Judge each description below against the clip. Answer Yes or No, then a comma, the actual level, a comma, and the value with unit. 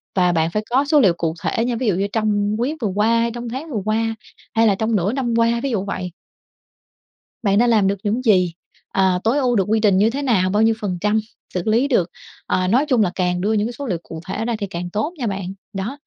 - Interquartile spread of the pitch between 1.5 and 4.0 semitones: Yes, average, 3.6 semitones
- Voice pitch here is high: Yes, high, 215 Hz